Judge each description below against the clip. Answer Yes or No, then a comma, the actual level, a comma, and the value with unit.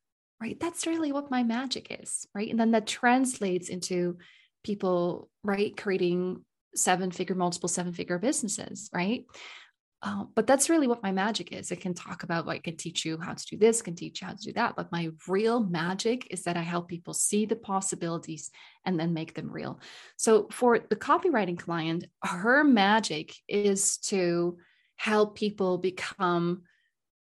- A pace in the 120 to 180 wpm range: Yes, average, 170 wpm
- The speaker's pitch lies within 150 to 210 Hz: Yes, high, 190 Hz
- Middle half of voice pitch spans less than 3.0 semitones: No, average, 4.2 semitones